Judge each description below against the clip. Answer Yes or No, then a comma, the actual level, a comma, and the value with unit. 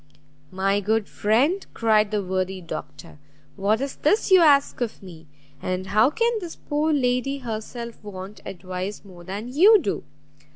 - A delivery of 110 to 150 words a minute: No, average, 160 wpm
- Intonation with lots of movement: Yes, wide, 6.6 semitones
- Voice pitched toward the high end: Yes, high, 215 Hz